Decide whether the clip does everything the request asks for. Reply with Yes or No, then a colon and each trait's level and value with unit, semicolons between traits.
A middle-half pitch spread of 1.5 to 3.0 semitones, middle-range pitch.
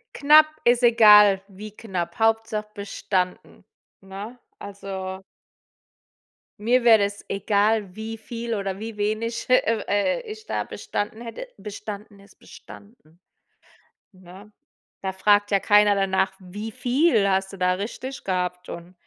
No: narrow, 2.6 semitones; high, 205 Hz